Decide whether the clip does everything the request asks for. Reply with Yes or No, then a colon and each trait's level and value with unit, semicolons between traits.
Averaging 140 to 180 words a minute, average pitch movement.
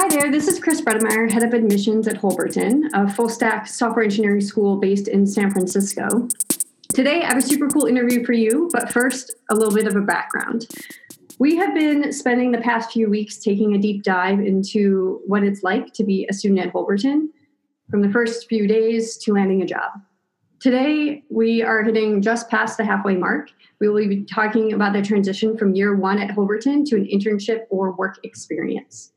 No: average, 195 wpm; average, 3.2 semitones